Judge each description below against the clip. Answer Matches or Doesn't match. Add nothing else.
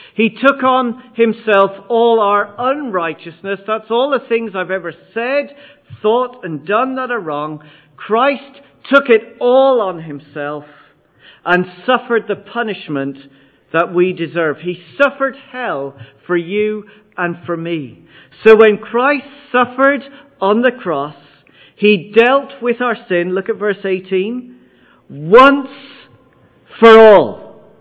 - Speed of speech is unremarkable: Doesn't match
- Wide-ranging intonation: Matches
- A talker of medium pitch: Doesn't match